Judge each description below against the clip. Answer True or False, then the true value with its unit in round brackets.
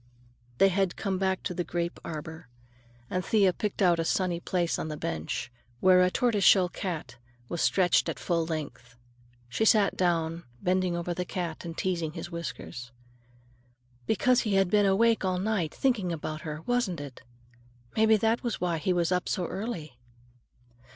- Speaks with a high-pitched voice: False (180 Hz)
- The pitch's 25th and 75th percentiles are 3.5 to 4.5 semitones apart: False (3.0 semitones)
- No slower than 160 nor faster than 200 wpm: True (175 wpm)